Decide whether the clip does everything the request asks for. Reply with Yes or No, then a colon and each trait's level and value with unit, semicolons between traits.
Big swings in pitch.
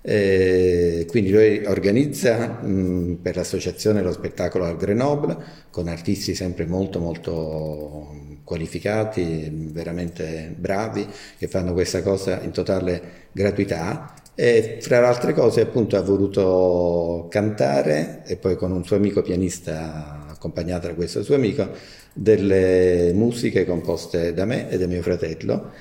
No: average, 2.7 semitones